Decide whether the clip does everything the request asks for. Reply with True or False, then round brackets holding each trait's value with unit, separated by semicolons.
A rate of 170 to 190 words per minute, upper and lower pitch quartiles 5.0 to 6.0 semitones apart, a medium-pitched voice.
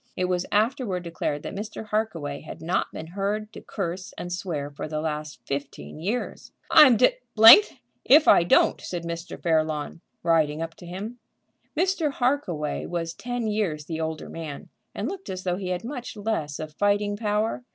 True (175 wpm; 5.3 semitones; 180 Hz)